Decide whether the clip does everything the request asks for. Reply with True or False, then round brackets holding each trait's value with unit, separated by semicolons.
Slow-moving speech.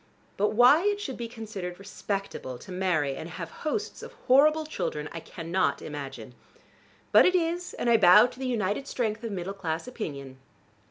False (175 wpm)